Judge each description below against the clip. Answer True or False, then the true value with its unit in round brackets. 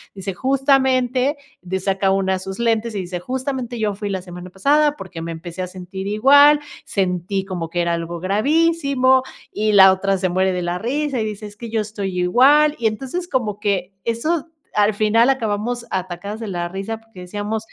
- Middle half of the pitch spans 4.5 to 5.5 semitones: True (5.2 semitones)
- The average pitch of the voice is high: True (210 Hz)